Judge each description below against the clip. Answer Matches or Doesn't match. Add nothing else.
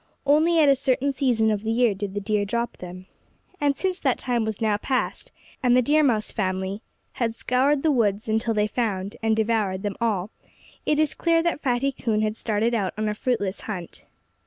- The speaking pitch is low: Doesn't match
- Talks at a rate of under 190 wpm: Doesn't match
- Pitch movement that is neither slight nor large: Matches